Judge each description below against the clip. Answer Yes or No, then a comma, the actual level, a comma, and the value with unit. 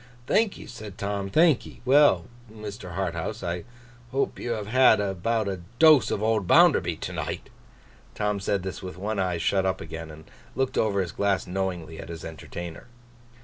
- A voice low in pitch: Yes, low, 100 Hz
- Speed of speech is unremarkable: Yes, average, 170 wpm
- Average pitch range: Yes, average, 3.8 semitones